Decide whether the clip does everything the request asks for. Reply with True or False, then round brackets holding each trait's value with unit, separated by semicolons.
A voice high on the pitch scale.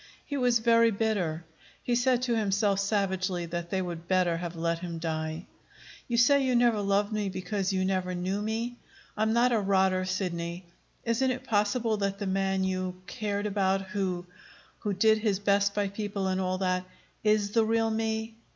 True (200 Hz)